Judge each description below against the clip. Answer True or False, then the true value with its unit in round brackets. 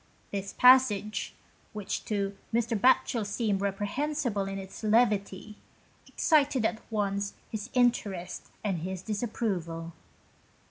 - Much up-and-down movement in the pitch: False (3.1 semitones)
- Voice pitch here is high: True (210 Hz)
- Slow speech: True (105 wpm)